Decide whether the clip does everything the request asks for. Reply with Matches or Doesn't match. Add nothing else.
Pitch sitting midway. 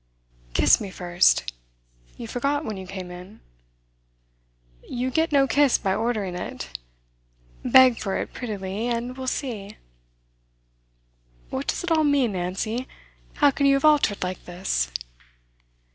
Doesn't match